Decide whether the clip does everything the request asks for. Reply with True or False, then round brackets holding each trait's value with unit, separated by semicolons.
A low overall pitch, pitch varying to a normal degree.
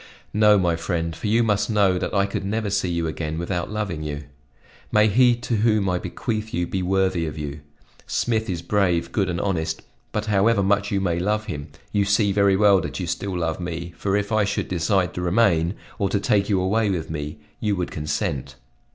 True (95 Hz; 3.5 semitones)